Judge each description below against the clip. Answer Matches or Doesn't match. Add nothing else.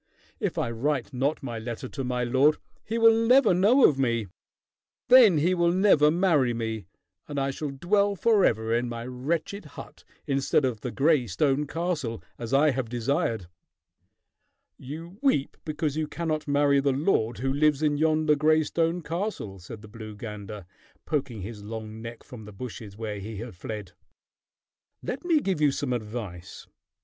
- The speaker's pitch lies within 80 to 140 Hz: Matches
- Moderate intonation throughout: Doesn't match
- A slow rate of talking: Doesn't match